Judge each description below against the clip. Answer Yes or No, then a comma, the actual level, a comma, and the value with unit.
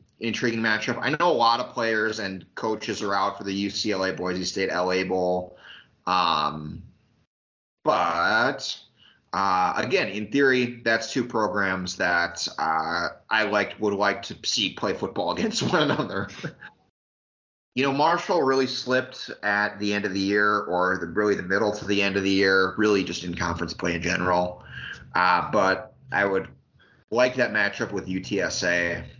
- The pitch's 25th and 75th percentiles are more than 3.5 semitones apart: No, average, 3.2 semitones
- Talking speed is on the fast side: No, average, 160 wpm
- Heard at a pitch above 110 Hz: No, low, 100 Hz